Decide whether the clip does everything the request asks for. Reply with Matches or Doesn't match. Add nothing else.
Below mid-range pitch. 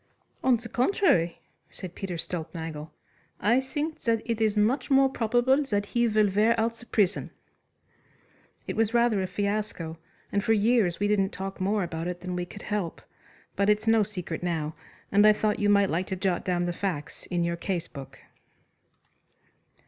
Doesn't match